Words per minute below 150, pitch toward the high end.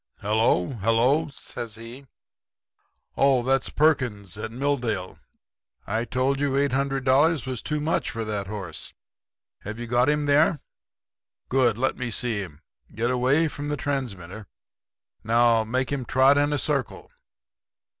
No: slow, 135 wpm; low, 125 Hz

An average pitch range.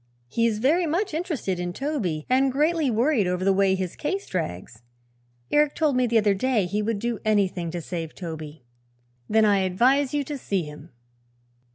No: wide, 7.2 semitones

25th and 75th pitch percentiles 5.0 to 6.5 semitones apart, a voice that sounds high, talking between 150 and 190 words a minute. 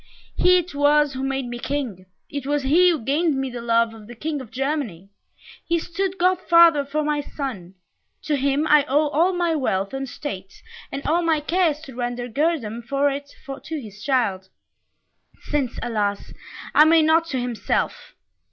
No: average, 4.5 semitones; very high, 280 Hz; average, 180 wpm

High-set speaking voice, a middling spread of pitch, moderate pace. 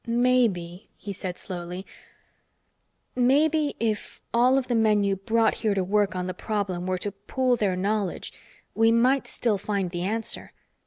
Yes: high, 210 Hz; average, 4.0 semitones; average, 160 wpm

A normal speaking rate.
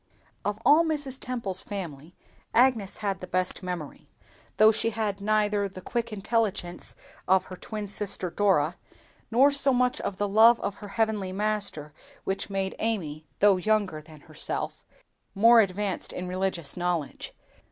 Yes: average, 150 wpm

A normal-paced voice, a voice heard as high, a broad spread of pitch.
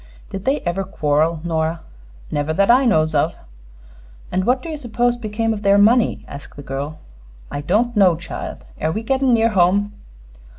Yes: average, 175 wpm; high, 200 Hz; wide, 6.7 semitones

